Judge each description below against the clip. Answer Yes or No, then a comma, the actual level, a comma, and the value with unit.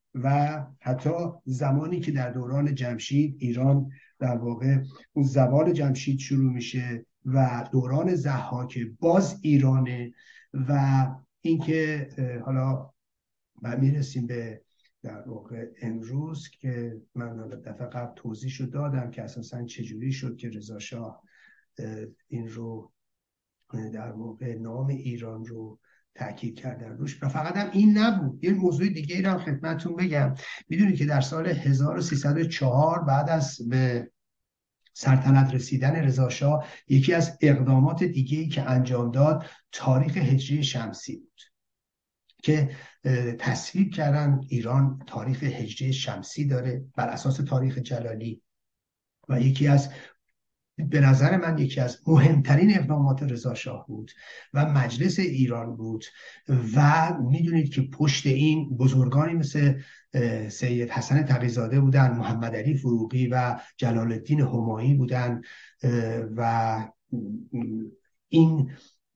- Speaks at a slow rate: No, average, 115 wpm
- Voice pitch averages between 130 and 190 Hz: Yes, low, 135 Hz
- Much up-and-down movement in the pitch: No, average, 3.2 semitones